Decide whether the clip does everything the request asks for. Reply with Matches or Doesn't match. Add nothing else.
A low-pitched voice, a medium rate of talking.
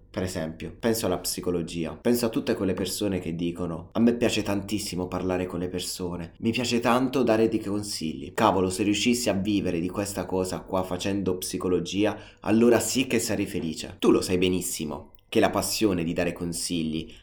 Doesn't match